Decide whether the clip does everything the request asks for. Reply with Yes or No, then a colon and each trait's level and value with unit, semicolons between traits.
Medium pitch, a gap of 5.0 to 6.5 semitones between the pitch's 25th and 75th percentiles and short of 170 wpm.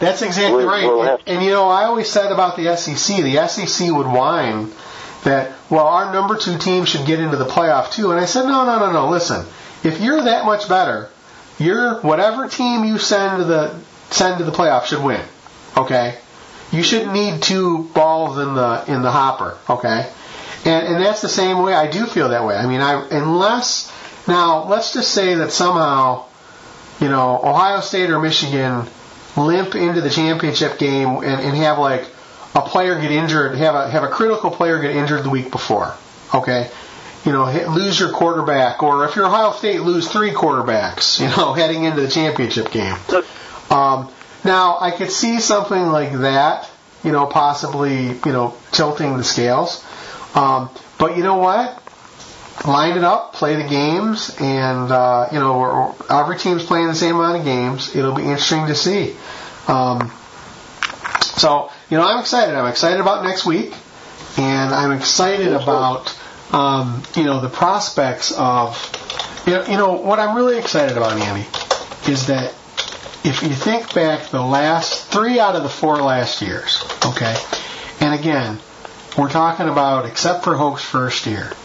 No: medium, 155 Hz; wide, 5.5 semitones; average, 180 wpm